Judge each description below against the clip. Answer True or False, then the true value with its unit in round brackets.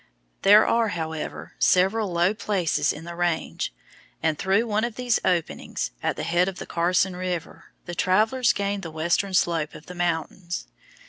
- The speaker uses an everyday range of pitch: True (3.1 semitones)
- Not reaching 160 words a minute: False (170 wpm)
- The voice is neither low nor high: True (180 Hz)